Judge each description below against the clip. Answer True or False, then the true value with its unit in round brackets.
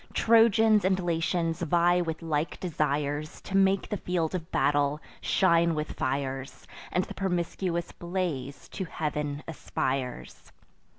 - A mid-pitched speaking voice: True (165 Hz)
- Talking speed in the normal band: False (125 wpm)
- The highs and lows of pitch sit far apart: False (3.7 semitones)